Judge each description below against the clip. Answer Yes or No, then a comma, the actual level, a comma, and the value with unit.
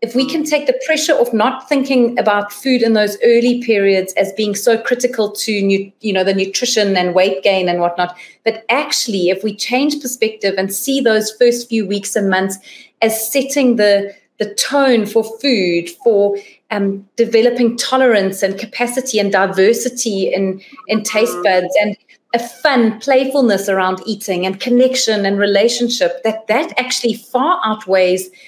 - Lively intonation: No, average, 3.8 semitones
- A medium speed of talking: Yes, average, 165 wpm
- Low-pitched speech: No, high, 220 Hz